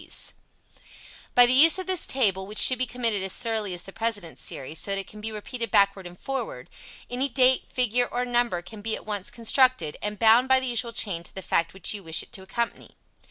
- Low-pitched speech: No, high, 225 Hz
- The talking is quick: Yes, fast, 230 wpm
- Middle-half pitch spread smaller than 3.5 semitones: No, average, 4.3 semitones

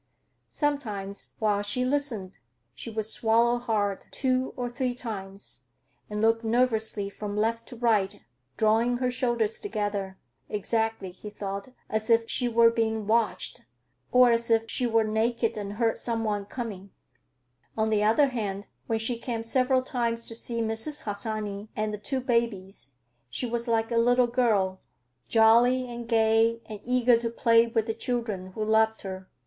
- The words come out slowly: No, average, 160 wpm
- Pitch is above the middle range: Yes, high, 225 Hz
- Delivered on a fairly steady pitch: Yes, narrow, 2.2 semitones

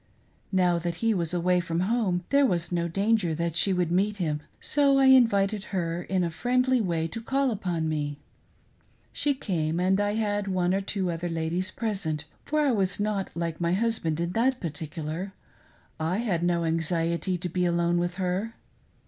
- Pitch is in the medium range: Yes, medium, 180 Hz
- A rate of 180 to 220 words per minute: Yes, average, 185 wpm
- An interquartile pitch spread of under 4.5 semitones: Yes, average, 3.7 semitones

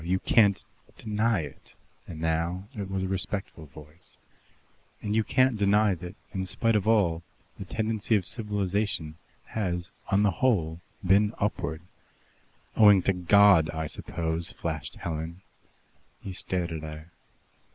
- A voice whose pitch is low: Yes, very low, 95 Hz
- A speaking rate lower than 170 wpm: Yes, average, 140 wpm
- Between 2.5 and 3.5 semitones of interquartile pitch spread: No, average, 4.1 semitones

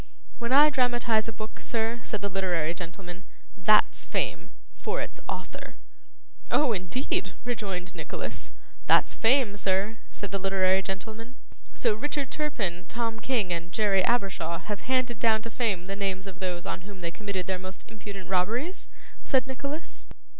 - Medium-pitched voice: No, high, 205 Hz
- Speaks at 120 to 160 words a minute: Yes, average, 155 wpm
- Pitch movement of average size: Yes, average, 4.1 semitones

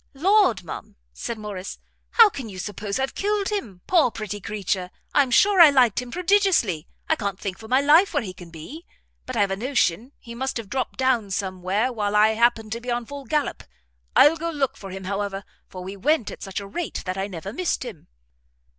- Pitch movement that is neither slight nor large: No, wide, 6.3 semitones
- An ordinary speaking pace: No, fast, 220 wpm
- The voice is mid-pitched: No, high, 225 Hz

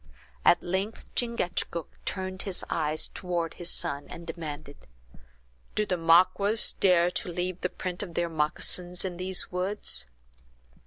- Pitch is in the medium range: Yes, medium, 180 Hz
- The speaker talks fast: No, average, 145 wpm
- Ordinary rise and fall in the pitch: No, narrow, 2.0 semitones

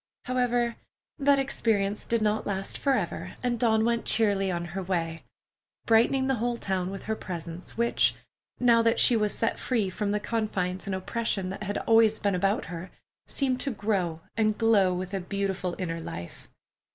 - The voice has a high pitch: Yes, high, 210 Hz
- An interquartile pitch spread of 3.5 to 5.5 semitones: Yes, average, 3.8 semitones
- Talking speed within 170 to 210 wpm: Yes, average, 175 wpm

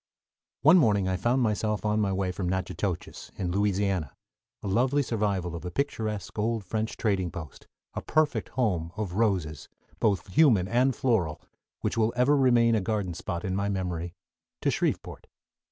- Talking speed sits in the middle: Yes, average, 165 wpm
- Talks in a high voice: No, low, 100 Hz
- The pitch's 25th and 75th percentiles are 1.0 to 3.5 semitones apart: No, average, 4.0 semitones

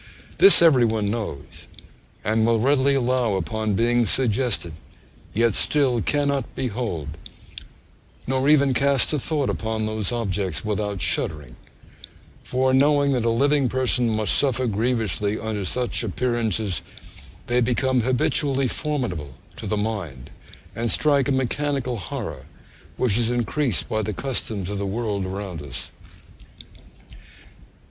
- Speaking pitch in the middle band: No, low, 115 Hz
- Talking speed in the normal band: No, slow, 130 wpm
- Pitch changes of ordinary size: Yes, average, 4.1 semitones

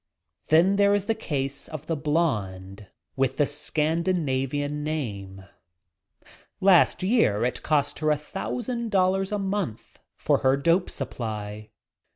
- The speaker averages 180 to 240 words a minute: No, average, 145 wpm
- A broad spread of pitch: Yes, wide, 6.7 semitones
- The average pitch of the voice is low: No, medium, 150 Hz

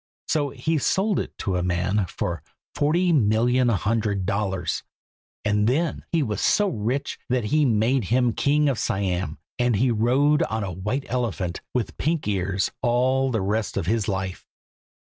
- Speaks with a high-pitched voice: No, low, 115 Hz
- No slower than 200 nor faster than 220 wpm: No, average, 165 wpm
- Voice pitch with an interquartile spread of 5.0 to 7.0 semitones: Yes, average, 5.3 semitones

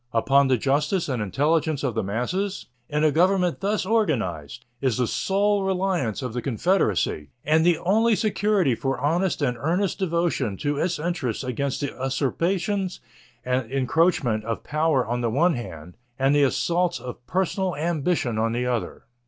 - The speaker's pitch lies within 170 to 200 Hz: No, medium, 145 Hz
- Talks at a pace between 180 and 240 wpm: No, average, 160 wpm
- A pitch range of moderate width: No, wide, 6.4 semitones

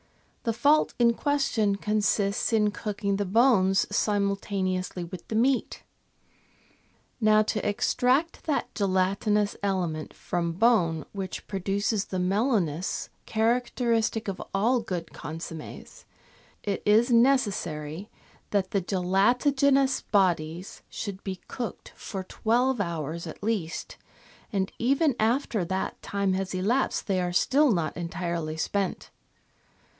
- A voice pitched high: Yes, high, 200 Hz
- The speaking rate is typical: No, slow, 120 wpm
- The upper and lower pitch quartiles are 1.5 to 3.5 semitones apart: No, average, 3.9 semitones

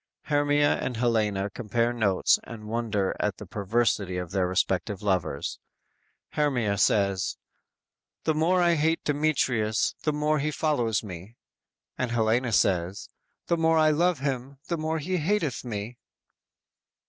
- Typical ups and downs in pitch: No, wide, 6.7 semitones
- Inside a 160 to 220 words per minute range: No, average, 140 wpm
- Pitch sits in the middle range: No, low, 120 Hz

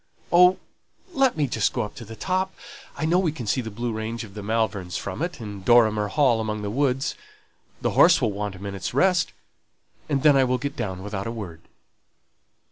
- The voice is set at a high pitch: No, low, 115 Hz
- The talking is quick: Yes, fast, 210 wpm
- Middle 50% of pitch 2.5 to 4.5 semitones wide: No, wide, 5.5 semitones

